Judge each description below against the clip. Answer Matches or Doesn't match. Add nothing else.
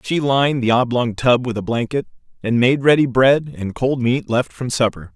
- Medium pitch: Doesn't match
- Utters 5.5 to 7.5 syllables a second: Doesn't match